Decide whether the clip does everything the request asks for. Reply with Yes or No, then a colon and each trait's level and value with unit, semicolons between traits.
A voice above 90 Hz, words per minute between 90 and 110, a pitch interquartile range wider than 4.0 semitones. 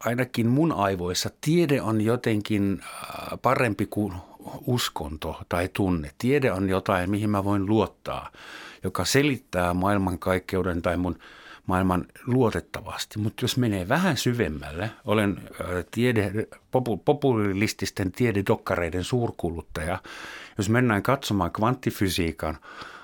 Yes: low, 105 Hz; average, 105 wpm; average, 4.5 semitones